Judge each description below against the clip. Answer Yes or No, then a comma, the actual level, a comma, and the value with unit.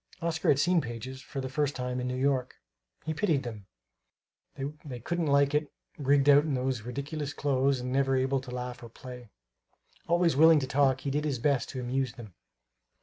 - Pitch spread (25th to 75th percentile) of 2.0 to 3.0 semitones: Yes, narrow, 2.5 semitones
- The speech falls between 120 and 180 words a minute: No, average, 195 wpm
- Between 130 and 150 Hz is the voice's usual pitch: Yes, low, 135 Hz